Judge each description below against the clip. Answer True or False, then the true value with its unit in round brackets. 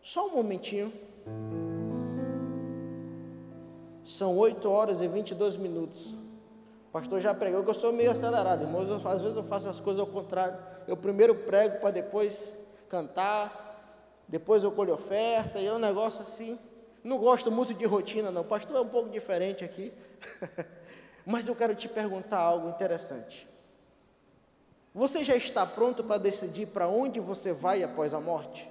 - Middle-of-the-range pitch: False (205 Hz)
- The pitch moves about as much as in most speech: True (3.4 semitones)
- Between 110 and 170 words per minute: True (160 wpm)